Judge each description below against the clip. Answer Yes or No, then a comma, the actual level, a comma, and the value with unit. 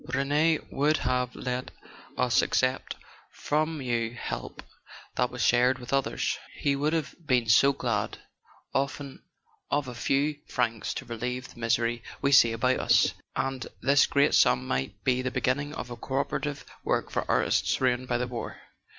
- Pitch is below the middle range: Yes, low, 130 Hz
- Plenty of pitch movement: No, narrow, 2.5 semitones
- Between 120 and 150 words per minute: No, average, 165 wpm